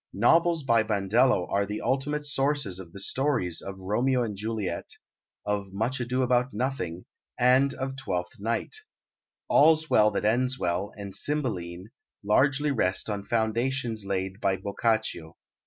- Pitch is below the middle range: Yes, low, 110 Hz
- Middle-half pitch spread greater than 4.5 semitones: Yes, average, 5.2 semitones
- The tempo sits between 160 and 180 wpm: No, average, 140 wpm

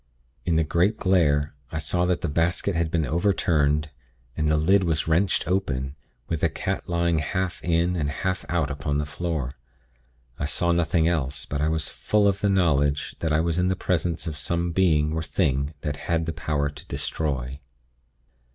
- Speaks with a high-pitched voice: No, very low, 80 Hz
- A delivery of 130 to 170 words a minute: No, average, 185 wpm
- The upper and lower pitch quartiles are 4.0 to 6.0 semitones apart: No, average, 2.8 semitones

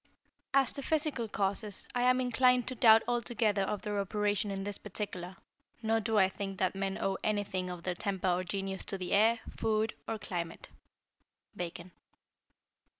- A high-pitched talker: Yes, high, 205 Hz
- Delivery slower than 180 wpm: Yes, average, 165 wpm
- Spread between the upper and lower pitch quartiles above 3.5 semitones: No, average, 2.7 semitones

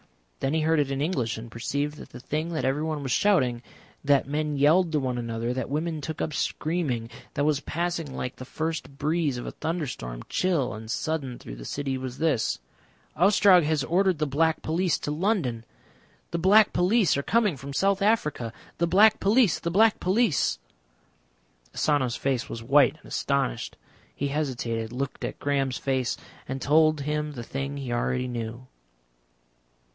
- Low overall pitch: No, medium, 145 Hz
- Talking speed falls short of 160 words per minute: No, average, 170 wpm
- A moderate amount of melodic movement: Yes, average, 4.3 semitones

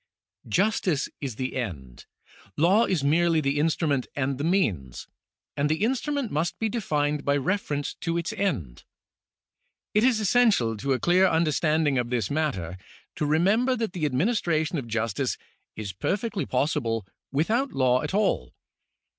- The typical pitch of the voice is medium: Yes, medium, 150 Hz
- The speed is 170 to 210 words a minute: No, average, 150 wpm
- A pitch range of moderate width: No, wide, 6.8 semitones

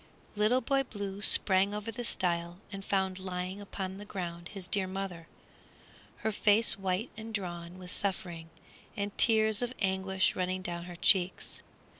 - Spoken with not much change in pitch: Yes, narrow, 2.3 semitones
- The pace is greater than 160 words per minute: No, average, 155 wpm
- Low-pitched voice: No, high, 190 Hz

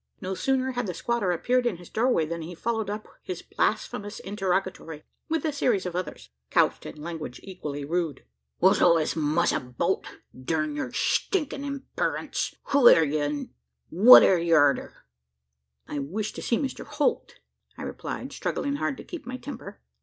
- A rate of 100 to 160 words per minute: No, average, 170 wpm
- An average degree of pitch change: No, wide, 7.4 semitones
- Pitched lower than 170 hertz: No, medium, 185 Hz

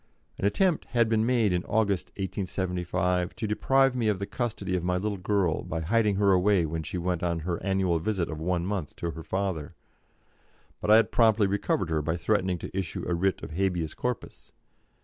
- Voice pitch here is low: Yes, very low, 95 Hz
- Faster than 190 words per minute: Yes, average, 200 wpm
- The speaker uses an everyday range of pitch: Yes, average, 3.4 semitones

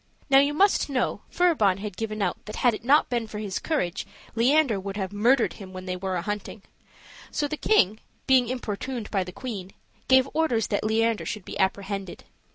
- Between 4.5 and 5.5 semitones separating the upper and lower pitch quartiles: Yes, average, 4.9 semitones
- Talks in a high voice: Yes, high, 215 Hz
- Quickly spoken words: No, average, 195 wpm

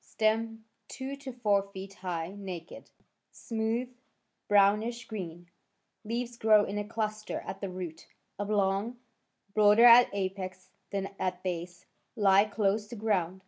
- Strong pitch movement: No, average, 2.9 semitones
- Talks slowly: Yes, slow, 130 wpm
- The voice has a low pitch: No, high, 205 Hz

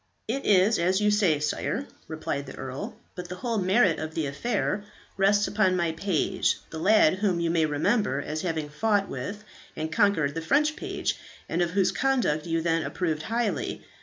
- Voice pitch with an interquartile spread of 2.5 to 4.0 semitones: No, average, 4.6 semitones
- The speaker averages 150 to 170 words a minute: No, average, 185 wpm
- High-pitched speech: No, medium, 180 Hz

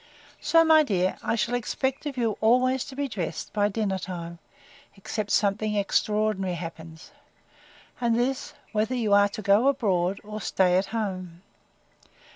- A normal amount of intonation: Yes, average, 4.3 semitones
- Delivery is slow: No, average, 150 wpm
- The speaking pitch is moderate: No, high, 210 Hz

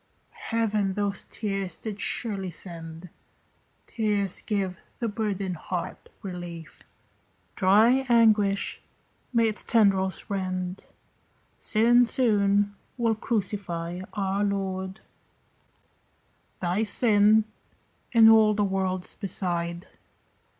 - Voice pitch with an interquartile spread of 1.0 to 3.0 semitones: Yes, average, 2.7 semitones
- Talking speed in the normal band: No, slow, 90 wpm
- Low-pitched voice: No, high, 200 Hz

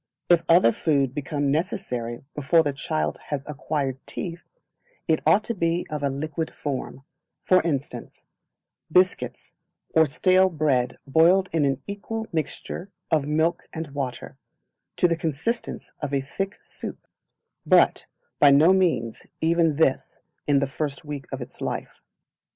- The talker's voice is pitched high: No, medium, 155 Hz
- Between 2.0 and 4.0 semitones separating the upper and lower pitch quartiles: Yes, average, 3.5 semitones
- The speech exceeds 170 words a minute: No, average, 145 wpm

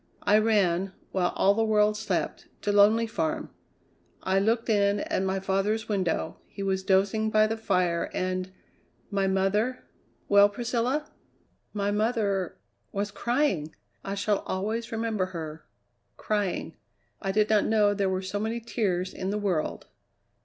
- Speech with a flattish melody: Yes, narrow, 2.3 semitones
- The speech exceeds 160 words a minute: No, average, 150 wpm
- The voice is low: No, high, 205 Hz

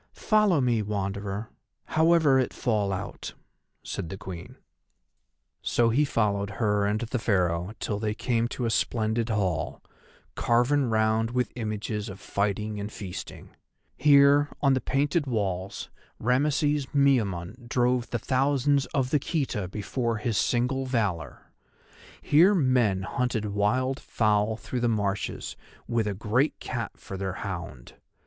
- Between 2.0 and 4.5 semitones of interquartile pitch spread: Yes, average, 4.2 semitones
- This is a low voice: Yes, low, 115 Hz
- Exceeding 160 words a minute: No, slow, 135 wpm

